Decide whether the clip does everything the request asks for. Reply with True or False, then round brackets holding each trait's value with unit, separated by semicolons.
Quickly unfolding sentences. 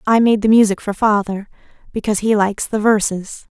False (185 wpm)